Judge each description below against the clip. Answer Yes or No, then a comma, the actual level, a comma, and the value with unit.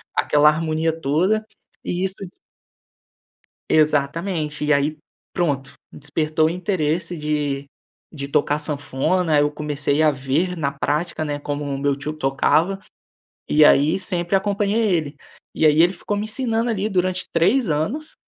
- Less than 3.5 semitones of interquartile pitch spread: No, average, 3.9 semitones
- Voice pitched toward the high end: No, medium, 155 Hz